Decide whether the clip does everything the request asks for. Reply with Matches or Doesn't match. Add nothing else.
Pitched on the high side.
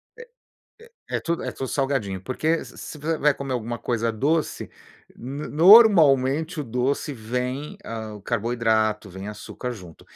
Doesn't match